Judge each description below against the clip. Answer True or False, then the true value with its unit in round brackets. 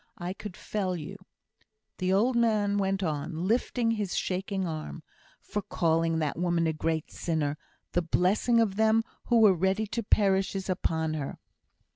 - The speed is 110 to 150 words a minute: False (160 wpm)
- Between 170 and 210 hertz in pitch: True (190 Hz)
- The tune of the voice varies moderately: True (4.2 semitones)